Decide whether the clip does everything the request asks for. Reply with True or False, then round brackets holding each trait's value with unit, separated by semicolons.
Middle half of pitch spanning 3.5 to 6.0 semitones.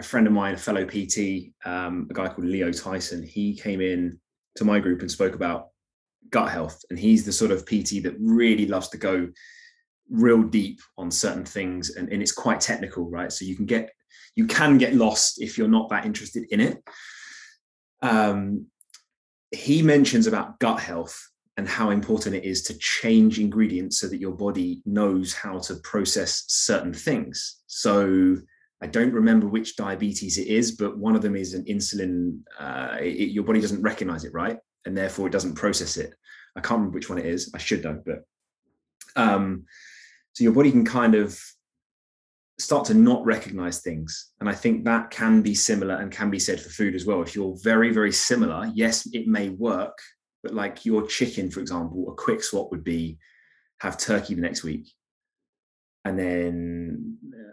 True (3.9 semitones)